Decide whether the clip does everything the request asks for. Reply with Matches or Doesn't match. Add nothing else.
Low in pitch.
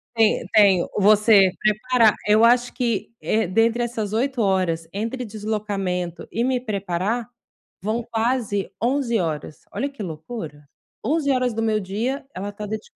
Doesn't match